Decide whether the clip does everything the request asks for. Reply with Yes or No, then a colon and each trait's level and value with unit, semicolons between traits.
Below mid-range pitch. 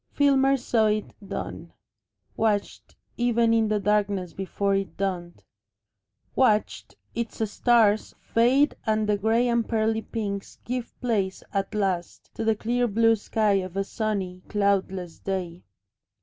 No: high, 215 Hz